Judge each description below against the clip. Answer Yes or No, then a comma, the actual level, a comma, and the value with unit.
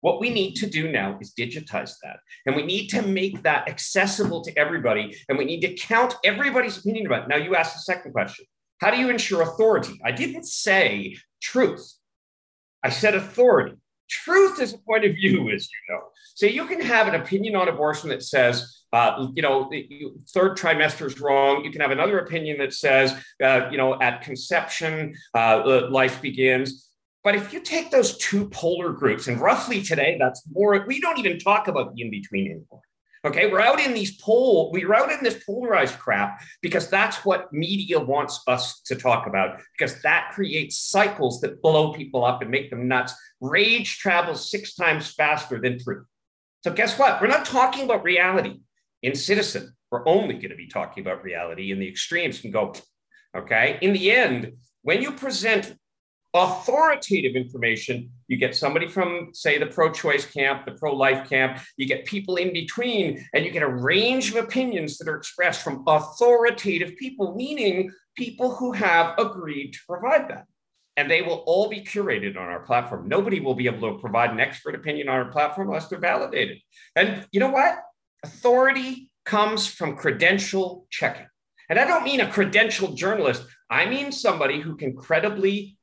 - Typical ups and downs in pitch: No, wide, 8.0 semitones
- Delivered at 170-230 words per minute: Yes, average, 185 wpm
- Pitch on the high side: No, medium, 175 Hz